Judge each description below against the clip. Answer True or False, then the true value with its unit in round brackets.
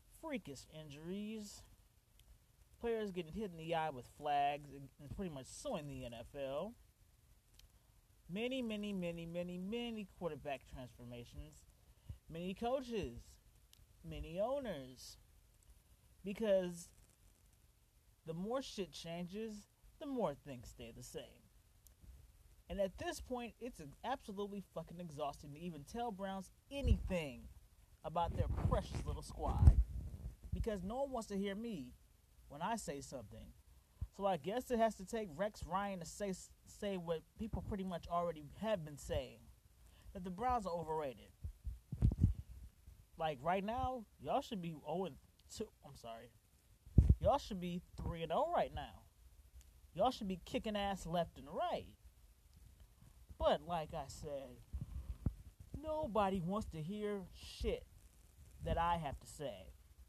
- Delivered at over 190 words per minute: False (135 wpm)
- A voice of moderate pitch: True (165 Hz)